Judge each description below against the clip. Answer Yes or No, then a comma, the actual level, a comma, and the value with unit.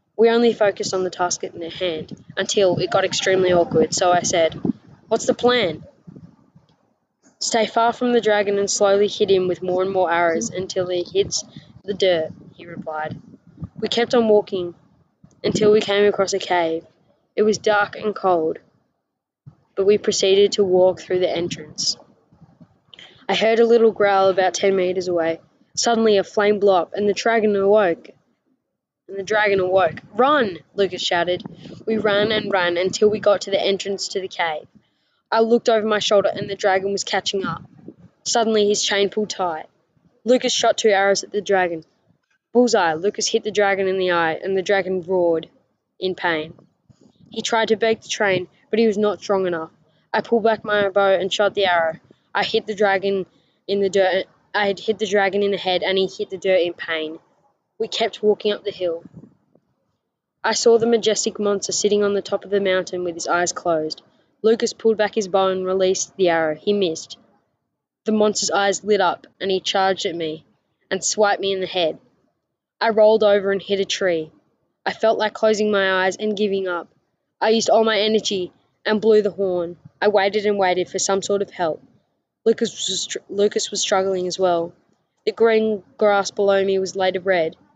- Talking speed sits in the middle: Yes, average, 190 wpm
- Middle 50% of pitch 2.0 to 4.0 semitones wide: Yes, narrow, 2.6 semitones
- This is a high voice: Yes, high, 195 Hz